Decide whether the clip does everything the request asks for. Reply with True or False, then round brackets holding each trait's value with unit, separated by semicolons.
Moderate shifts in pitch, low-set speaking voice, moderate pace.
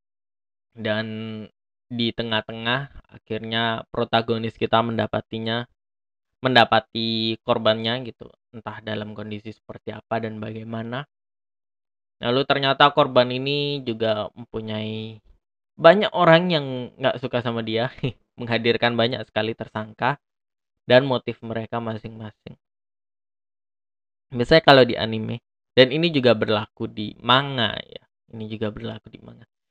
False (2.1 semitones; 115 Hz; 110 wpm)